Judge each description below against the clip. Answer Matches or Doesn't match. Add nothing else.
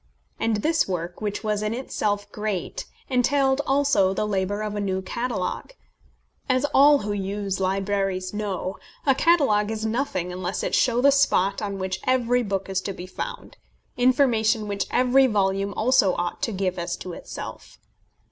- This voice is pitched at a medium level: Doesn't match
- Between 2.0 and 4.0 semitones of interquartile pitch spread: Doesn't match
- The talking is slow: Doesn't match